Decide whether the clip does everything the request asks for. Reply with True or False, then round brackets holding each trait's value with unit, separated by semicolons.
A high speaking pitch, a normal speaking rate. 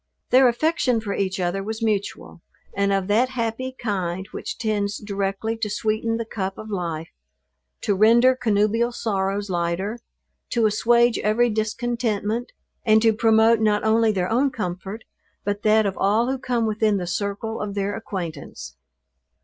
True (215 Hz; 155 wpm)